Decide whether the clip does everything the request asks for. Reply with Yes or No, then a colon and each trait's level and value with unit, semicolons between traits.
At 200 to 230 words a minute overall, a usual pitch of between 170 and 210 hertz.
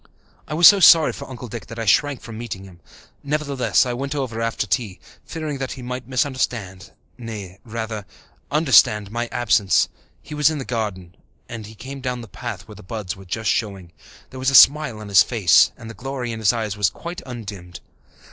No: fast, 205 wpm; low, 115 Hz